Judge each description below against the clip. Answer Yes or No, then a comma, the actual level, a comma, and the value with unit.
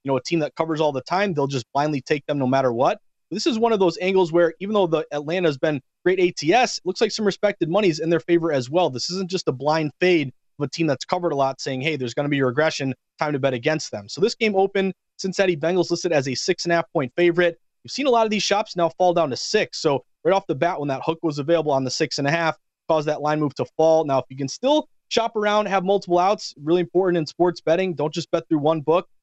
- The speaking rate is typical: No, fast, 290 wpm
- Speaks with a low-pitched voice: No, medium, 165 Hz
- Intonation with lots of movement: No, average, 3.8 semitones